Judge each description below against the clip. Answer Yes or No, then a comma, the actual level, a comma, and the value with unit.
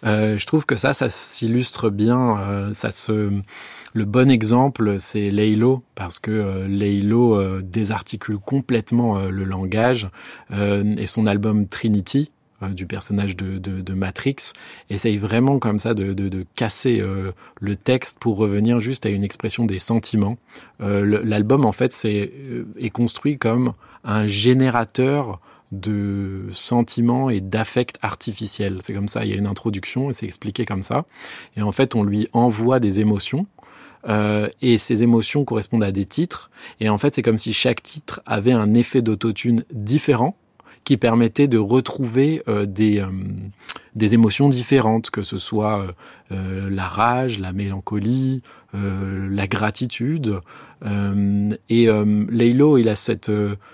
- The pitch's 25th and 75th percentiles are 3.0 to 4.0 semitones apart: Yes, average, 3.3 semitones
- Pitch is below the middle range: Yes, low, 110 Hz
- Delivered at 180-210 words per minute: No, average, 165 wpm